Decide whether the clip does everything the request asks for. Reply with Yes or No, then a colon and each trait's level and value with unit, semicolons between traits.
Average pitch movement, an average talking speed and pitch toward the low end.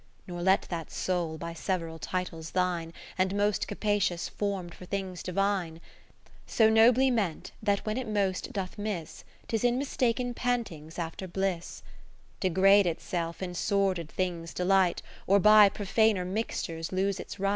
No: average, 3.0 semitones; average, 155 wpm; high, 190 Hz